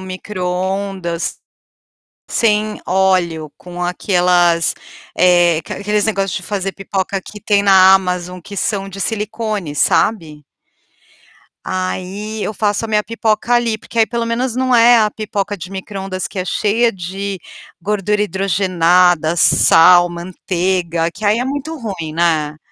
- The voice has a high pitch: Yes, high, 195 Hz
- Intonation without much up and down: No, average, 3.0 semitones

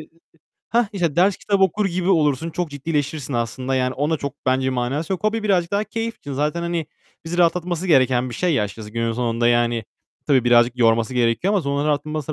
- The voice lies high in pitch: No, medium, 145 Hz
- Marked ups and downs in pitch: Yes, wide, 5.9 semitones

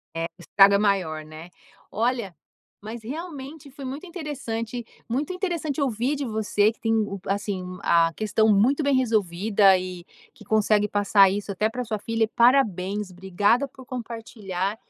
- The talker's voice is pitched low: No, high, 220 Hz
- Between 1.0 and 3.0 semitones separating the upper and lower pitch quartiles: No, average, 4.5 semitones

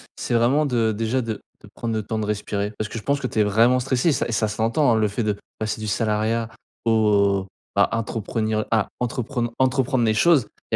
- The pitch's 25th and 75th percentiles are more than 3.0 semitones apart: No, narrow, 2.4 semitones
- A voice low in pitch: Yes, low, 115 Hz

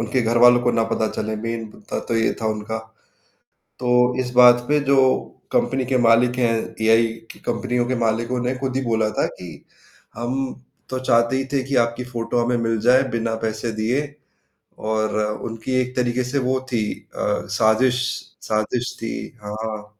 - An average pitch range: No, narrow, 2.1 semitones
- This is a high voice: No, low, 120 Hz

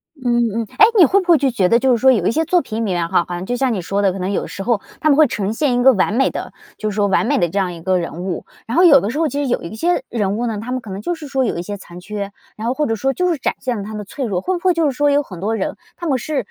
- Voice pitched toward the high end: Yes, high, 230 Hz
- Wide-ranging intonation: Yes, wide, 5.8 semitones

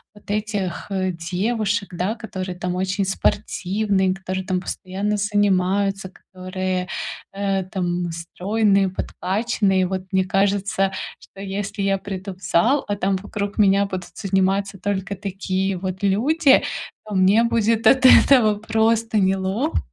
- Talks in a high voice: Yes, high, 195 Hz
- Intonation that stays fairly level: Yes, narrow, 1.8 semitones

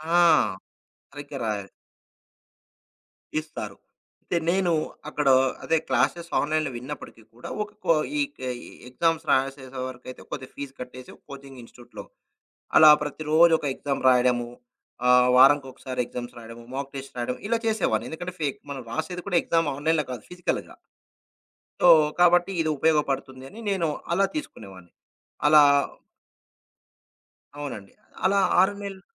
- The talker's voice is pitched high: No, medium, 145 Hz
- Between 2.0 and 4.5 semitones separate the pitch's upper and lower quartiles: No, average, 4.9 semitones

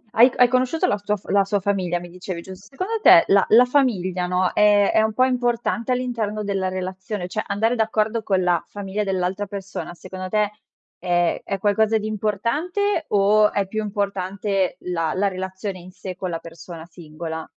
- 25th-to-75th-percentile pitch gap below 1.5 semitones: No, average, 2.9 semitones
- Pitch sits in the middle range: No, high, 200 Hz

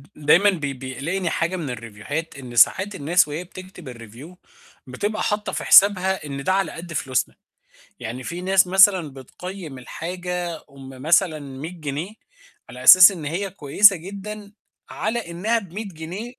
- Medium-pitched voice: Yes, medium, 175 Hz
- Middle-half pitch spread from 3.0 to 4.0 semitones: No, average, 5.3 semitones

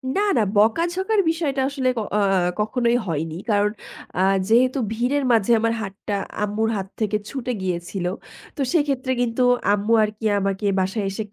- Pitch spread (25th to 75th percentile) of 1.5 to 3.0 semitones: No, average, 4.7 semitones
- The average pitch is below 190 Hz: No, high, 225 Hz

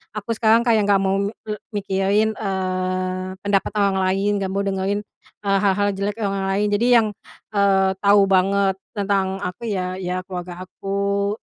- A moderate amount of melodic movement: No, narrow, 1.3 semitones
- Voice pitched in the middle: No, high, 195 Hz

